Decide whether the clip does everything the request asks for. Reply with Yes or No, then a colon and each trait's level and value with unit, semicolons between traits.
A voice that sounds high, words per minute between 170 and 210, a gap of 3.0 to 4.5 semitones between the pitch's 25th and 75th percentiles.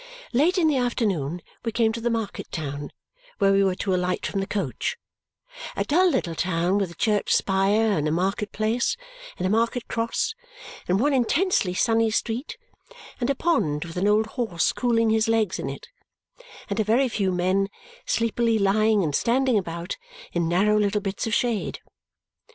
Yes: high, 210 Hz; average, 175 wpm; average, 3.9 semitones